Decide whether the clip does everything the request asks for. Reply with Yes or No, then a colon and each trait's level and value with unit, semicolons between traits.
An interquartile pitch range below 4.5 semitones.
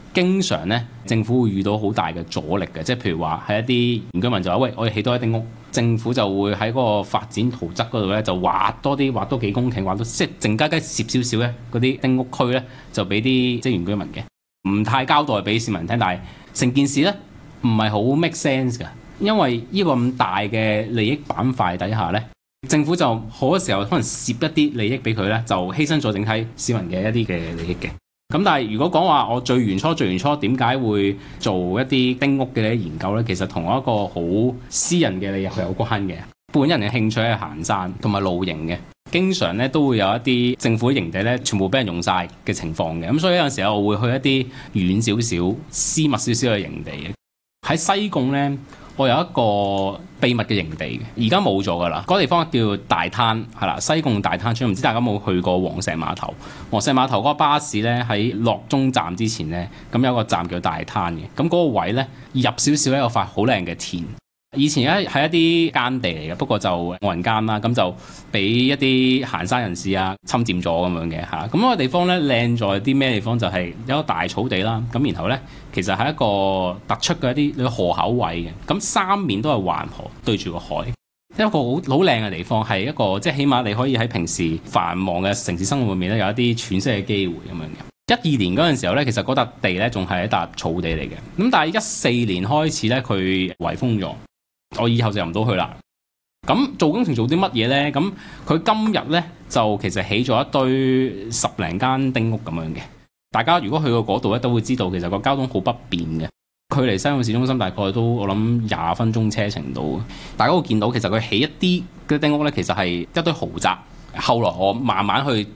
No: average, 5.2 semitones